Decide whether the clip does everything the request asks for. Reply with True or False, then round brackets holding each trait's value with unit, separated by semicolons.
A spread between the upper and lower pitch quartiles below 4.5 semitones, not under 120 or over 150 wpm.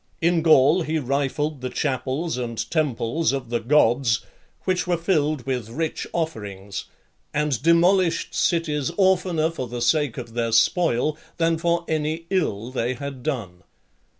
False (5.2 semitones; 145 wpm)